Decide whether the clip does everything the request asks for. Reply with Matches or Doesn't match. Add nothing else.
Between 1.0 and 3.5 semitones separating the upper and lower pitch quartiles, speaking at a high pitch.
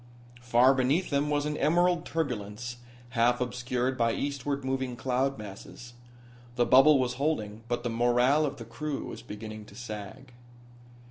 Doesn't match